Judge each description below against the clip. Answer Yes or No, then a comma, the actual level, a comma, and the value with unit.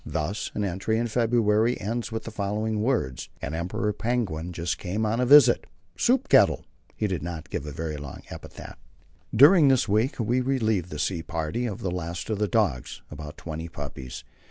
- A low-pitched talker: Yes, low, 105 Hz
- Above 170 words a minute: Yes, average, 185 wpm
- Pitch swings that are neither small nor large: No, wide, 5.9 semitones